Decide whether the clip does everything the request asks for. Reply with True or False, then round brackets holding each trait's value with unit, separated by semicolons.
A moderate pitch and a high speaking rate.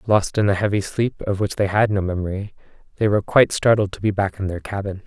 False (100 Hz; 250 wpm)